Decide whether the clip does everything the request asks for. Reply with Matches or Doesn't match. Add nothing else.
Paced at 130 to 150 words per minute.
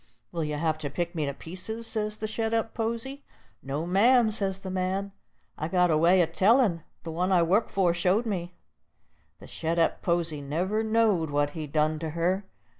Doesn't match